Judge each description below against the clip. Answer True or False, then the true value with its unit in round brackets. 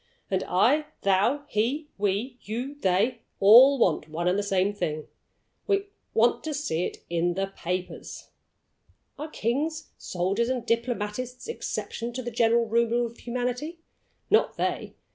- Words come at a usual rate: True (145 wpm)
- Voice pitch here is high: True (235 Hz)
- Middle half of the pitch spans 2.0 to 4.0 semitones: False (4.8 semitones)